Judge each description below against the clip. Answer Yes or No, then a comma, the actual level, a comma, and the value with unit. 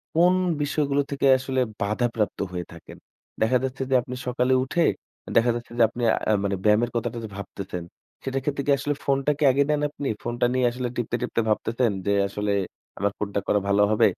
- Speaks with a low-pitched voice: Yes, low, 120 Hz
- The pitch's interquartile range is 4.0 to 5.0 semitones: Yes, average, 4.4 semitones